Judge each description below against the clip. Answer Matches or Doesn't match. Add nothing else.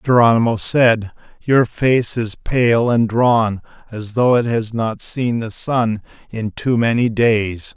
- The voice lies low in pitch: Matches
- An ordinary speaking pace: Matches